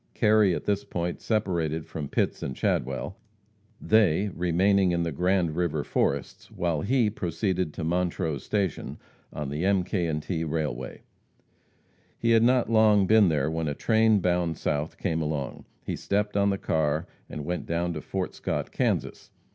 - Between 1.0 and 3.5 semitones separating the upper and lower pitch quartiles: No, average, 4.2 semitones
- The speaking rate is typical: Yes, average, 165 wpm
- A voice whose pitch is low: Yes, very low, 85 Hz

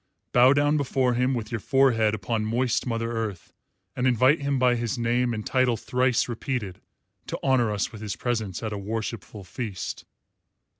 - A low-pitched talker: Yes, low, 120 Hz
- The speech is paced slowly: No, average, 170 wpm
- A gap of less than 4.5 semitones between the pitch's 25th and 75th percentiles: Yes, average, 2.8 semitones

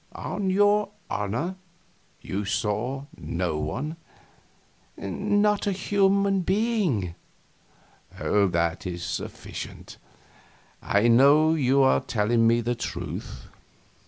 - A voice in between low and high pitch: No, low, 130 Hz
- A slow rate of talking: Yes, slow, 95 wpm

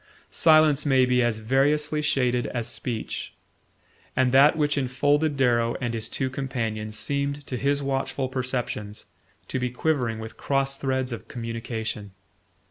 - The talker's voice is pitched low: Yes, low, 130 Hz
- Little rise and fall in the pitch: No, average, 3.1 semitones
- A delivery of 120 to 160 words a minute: Yes, average, 140 wpm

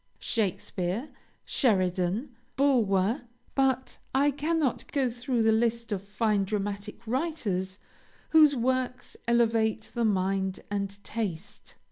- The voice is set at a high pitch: Yes, high, 225 Hz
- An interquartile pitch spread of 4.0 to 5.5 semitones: Yes, average, 4.6 semitones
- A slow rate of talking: Yes, slow, 105 wpm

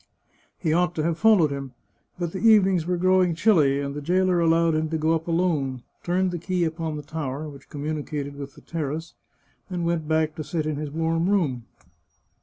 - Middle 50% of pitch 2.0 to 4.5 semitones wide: Yes, average, 2.9 semitones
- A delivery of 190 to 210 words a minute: Yes, average, 200 wpm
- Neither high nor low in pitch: Yes, medium, 160 Hz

